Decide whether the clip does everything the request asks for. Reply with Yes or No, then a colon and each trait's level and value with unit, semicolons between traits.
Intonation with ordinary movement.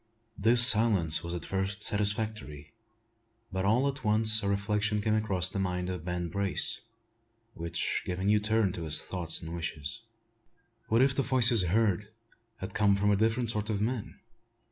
Yes: average, 3.4 semitones